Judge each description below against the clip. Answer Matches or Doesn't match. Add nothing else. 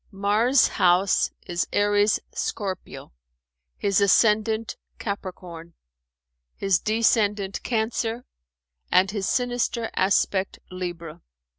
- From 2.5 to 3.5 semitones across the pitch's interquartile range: Matches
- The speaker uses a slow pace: Matches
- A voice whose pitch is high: Matches